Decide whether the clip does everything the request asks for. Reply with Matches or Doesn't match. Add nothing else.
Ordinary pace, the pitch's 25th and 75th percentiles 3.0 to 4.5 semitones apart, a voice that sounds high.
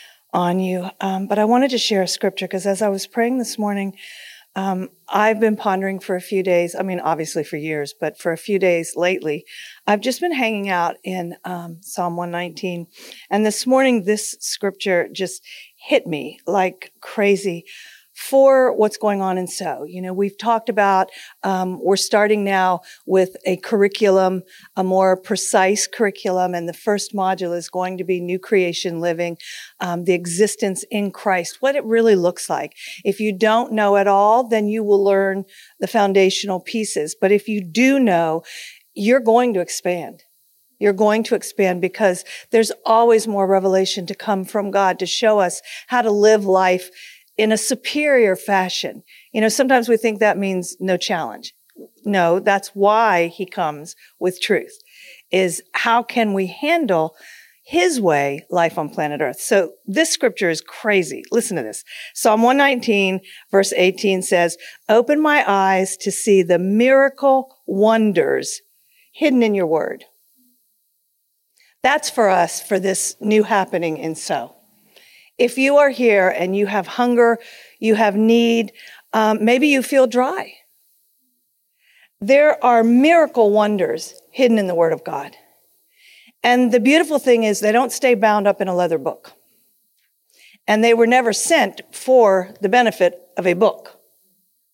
Matches